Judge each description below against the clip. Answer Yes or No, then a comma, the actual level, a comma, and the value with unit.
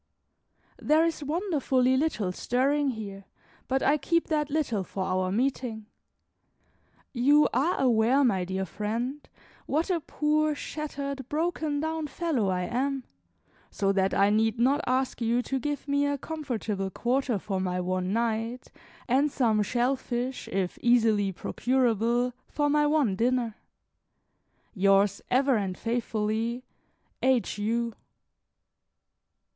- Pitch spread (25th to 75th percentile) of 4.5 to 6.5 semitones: Yes, average, 5.1 semitones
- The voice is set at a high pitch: Yes, high, 245 Hz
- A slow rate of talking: Yes, slow, 130 wpm